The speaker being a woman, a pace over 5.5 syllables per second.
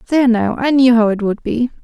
Yes: female; 5.9 syllables/s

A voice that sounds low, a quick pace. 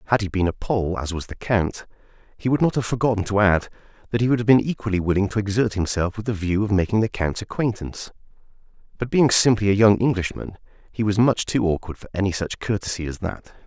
Yes: low, 105 Hz; fast, 225 wpm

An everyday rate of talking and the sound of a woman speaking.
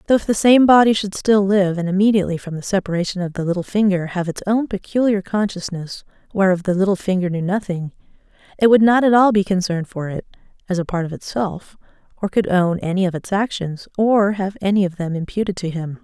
No: fast, 215 wpm; female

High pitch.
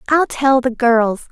Yes: very high, 250 Hz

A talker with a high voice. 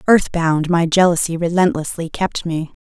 No: medium, 170 Hz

